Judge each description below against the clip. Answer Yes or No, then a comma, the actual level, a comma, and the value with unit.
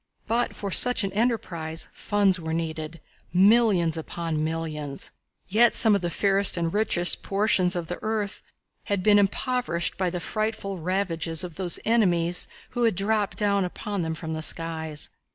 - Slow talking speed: No, average, 160 wpm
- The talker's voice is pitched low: No, medium, 185 Hz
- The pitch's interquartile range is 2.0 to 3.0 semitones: No, average, 3.9 semitones